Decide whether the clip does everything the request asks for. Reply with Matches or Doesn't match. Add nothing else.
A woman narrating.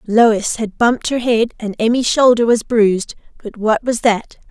Matches